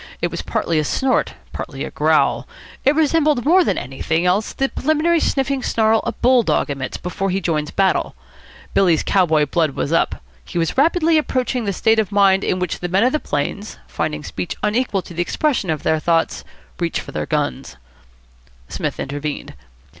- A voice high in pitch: Yes, high, 195 Hz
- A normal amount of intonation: No, wide, 8.3 semitones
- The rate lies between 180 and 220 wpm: Yes, average, 185 wpm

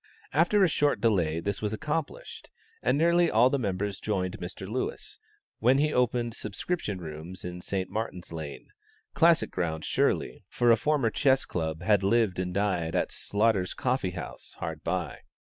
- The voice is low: Yes, low, 105 Hz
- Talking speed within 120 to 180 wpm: Yes, average, 160 wpm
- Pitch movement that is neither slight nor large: No, wide, 6.1 semitones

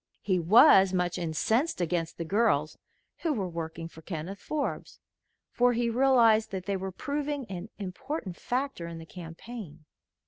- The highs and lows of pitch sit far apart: Yes, wide, 6.2 semitones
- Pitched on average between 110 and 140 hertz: No, high, 190 Hz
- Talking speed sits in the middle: Yes, average, 150 wpm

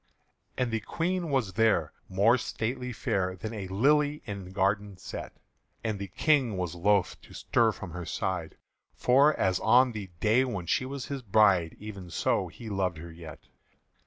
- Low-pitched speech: Yes, low, 105 Hz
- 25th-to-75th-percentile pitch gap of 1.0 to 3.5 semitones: No, average, 5.1 semitones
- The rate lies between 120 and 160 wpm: No, average, 170 wpm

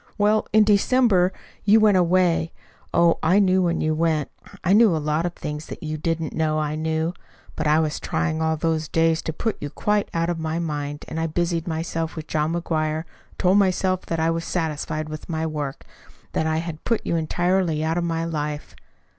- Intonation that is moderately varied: No, narrow, 2.1 semitones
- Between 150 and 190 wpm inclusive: No, fast, 205 wpm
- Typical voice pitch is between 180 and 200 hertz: No, medium, 165 Hz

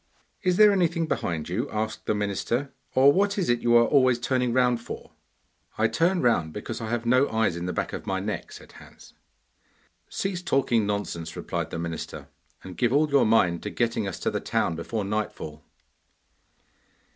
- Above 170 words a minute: Yes, average, 185 wpm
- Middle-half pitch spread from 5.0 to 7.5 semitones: Yes, average, 5.3 semitones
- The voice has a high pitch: No, low, 115 Hz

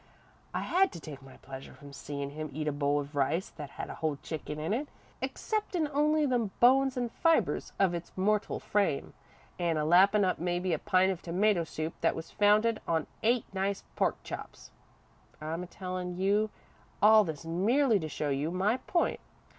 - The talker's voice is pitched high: No, medium, 180 Hz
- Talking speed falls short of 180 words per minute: No, average, 185 wpm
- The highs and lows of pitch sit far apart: Yes, wide, 5.7 semitones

